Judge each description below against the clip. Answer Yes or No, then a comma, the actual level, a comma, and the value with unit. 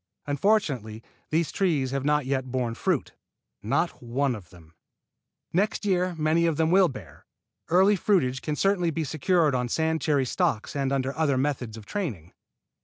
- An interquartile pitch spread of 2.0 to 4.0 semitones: No, average, 4.7 semitones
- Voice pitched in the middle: Yes, medium, 145 Hz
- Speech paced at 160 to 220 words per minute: Yes, average, 165 wpm